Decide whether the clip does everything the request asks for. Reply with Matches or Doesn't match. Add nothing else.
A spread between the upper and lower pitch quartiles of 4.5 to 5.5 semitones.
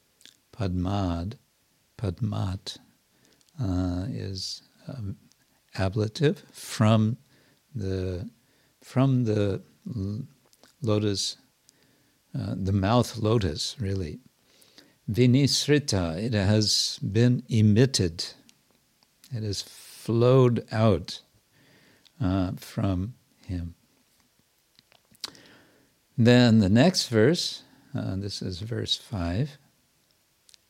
Matches